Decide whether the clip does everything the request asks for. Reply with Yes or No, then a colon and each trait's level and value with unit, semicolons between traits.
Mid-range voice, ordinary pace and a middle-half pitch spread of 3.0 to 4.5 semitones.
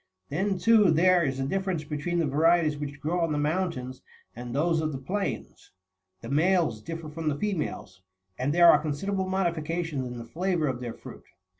Yes: medium, 160 Hz; average, 190 wpm; average, 3.9 semitones